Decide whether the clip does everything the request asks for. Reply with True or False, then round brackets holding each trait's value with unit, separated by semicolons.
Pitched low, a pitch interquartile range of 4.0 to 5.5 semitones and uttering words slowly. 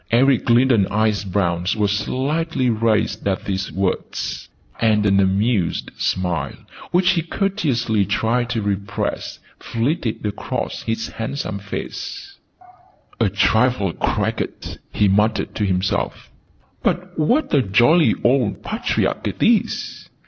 True (110 Hz; 4.4 semitones; 120 wpm)